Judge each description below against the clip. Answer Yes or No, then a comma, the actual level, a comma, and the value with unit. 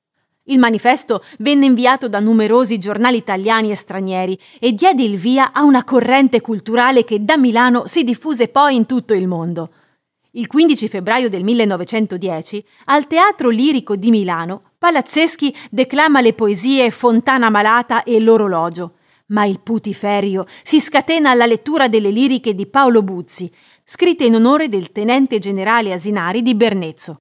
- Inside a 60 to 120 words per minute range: No, average, 150 wpm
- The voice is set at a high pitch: Yes, high, 230 Hz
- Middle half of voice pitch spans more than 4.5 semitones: No, average, 4.2 semitones